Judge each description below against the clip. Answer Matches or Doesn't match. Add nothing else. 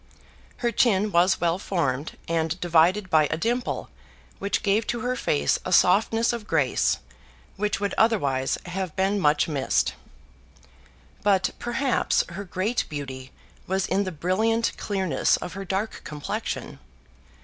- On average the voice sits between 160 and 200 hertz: Matches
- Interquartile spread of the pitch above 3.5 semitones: Matches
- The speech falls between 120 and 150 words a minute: Matches